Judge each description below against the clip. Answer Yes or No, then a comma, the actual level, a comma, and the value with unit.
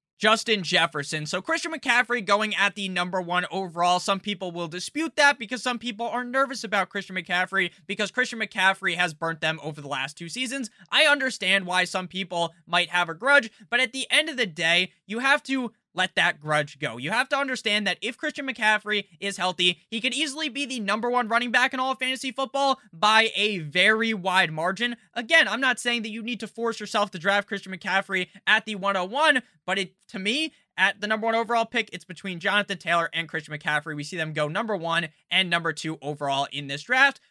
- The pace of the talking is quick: Yes, fast, 215 wpm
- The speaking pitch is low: No, high, 200 Hz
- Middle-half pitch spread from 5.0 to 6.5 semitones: Yes, wide, 5.4 semitones